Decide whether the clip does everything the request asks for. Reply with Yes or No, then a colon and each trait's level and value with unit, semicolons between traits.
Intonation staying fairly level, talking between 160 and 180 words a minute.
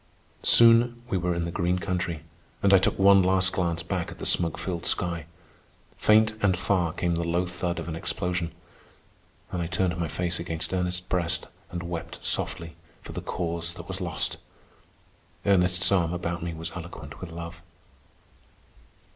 Yes: narrow, 1.6 semitones; average, 170 wpm